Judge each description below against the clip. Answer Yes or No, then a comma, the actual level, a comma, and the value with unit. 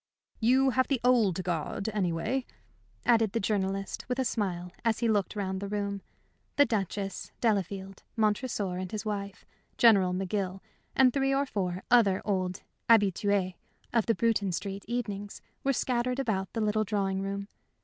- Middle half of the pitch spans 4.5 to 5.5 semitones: No, average, 3.3 semitones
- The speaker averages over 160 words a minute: No, average, 155 wpm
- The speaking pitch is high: Yes, high, 205 Hz